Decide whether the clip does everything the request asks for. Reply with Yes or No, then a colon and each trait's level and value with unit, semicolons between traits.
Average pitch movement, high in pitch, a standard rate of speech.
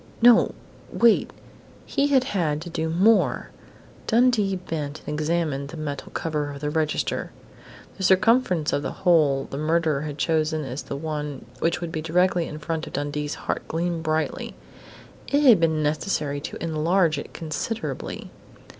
No: average, 3.2 semitones; medium, 160 Hz; average, 155 wpm